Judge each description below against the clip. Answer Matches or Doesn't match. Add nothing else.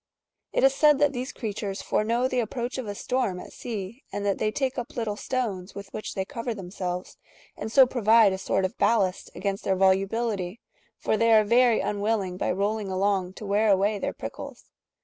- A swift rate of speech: Matches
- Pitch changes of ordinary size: Matches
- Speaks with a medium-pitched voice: Doesn't match